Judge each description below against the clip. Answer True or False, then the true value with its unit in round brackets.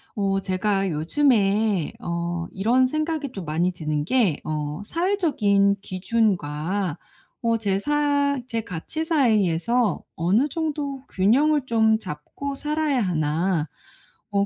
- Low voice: False (205 Hz)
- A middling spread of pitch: False (7.7 semitones)